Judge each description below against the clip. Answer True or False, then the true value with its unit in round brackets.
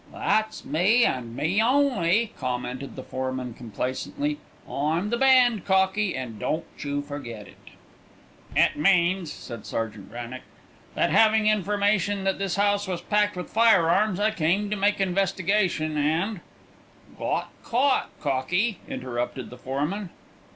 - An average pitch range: False (7.4 semitones)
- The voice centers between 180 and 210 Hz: True (185 Hz)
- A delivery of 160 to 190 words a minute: False (135 wpm)